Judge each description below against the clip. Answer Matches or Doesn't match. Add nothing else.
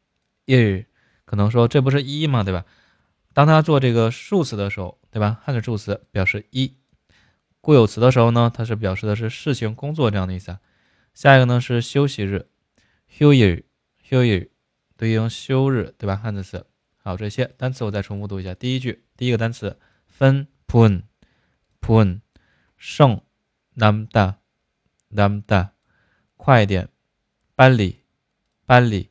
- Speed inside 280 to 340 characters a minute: Doesn't match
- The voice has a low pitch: Matches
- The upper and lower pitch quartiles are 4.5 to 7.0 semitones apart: Doesn't match